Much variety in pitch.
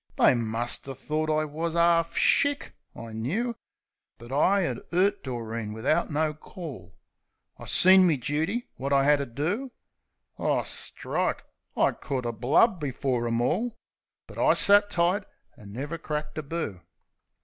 Yes: wide, 5.9 semitones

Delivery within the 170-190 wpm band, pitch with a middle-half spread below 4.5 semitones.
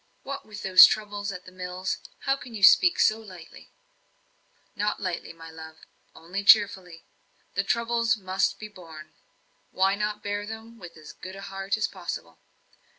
No: average, 150 wpm; average, 2.9 semitones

